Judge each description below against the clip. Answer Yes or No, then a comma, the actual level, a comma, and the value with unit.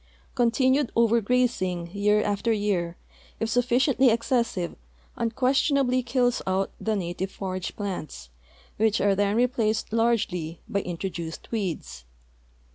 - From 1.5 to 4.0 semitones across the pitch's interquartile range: No, average, 4.4 semitones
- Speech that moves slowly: Yes, slow, 120 wpm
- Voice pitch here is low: No, high, 215 Hz